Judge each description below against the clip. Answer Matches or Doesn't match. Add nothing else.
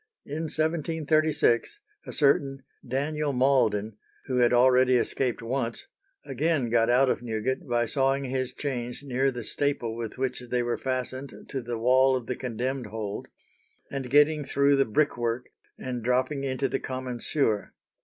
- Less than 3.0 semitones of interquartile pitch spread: Matches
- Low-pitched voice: Matches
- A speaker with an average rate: Matches